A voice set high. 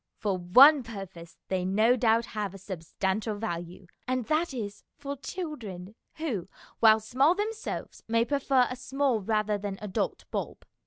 Yes: high, 220 Hz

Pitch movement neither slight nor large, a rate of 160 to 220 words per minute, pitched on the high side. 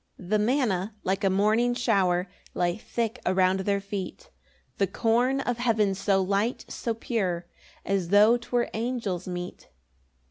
No: average, 3.8 semitones; average, 145 wpm; high, 205 Hz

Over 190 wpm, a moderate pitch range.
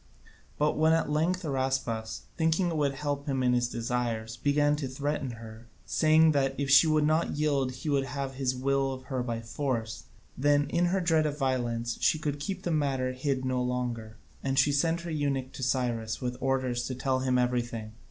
Yes: average, 200 wpm; average, 3.0 semitones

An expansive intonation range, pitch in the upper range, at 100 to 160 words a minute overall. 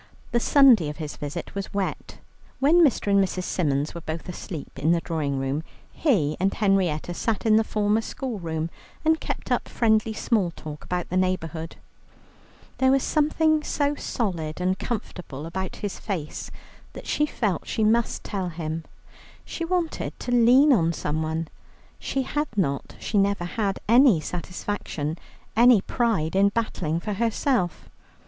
Yes: wide, 6.3 semitones; high, 195 Hz; average, 155 wpm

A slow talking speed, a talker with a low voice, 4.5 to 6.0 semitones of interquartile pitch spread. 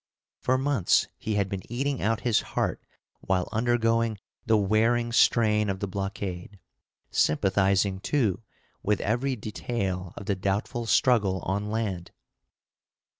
No: slow, 125 wpm; low, 105 Hz; average, 3.3 semitones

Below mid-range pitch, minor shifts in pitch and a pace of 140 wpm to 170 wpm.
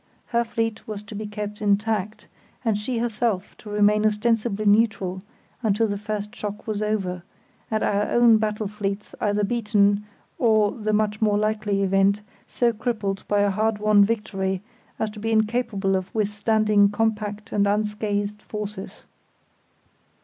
No: high, 210 Hz; narrow, 1.2 semitones; average, 150 wpm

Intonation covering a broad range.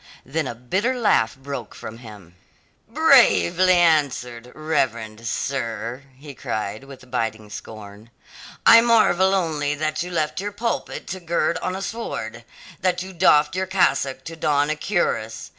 Yes: wide, 7.5 semitones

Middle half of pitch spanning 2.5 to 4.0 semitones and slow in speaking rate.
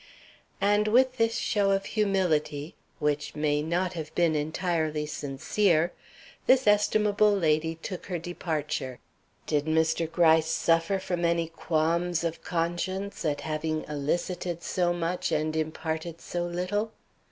Yes: average, 3.0 semitones; slow, 130 wpm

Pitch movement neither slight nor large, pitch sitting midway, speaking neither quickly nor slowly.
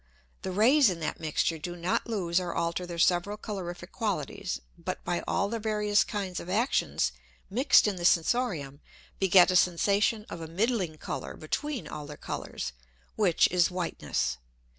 Yes: average, 3.8 semitones; medium, 180 Hz; average, 160 wpm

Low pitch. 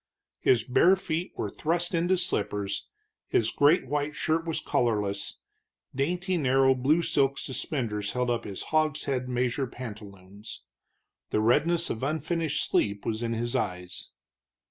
Yes: low, 130 Hz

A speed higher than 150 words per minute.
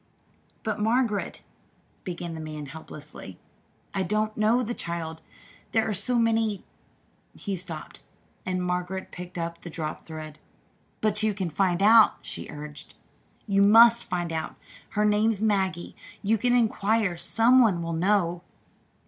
No: average, 145 wpm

